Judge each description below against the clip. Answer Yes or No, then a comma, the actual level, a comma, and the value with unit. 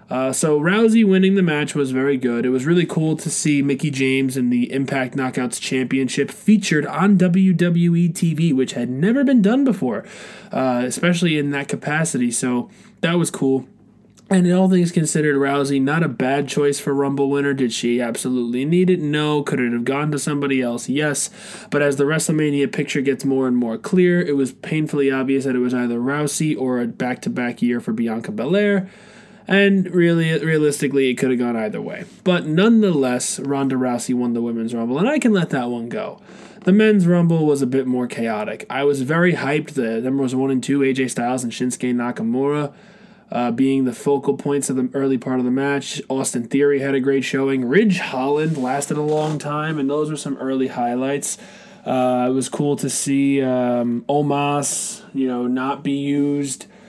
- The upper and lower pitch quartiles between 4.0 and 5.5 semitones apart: Yes, average, 4.5 semitones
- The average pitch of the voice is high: No, medium, 140 Hz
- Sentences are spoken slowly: No, average, 195 wpm